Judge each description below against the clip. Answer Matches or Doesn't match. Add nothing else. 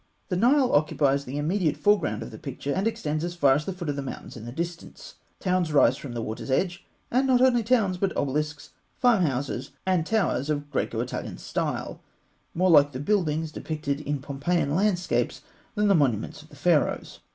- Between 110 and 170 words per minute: Doesn't match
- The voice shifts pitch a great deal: Doesn't match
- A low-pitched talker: Doesn't match